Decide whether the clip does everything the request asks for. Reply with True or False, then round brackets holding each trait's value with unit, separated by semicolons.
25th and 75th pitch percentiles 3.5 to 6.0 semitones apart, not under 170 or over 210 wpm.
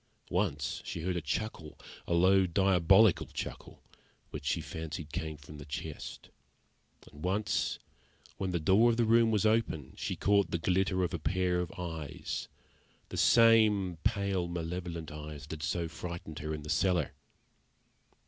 False (3.8 semitones; 160 wpm)